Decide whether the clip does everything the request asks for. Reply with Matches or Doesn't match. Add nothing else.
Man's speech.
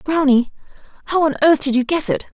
Doesn't match